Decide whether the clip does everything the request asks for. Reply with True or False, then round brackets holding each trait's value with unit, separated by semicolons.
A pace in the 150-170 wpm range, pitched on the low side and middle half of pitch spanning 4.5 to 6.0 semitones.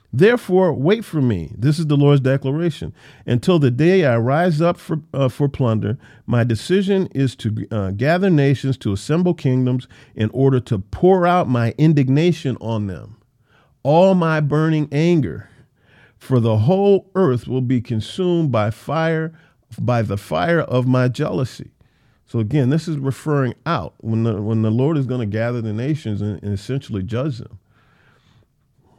True (165 wpm; 130 Hz; 5.6 semitones)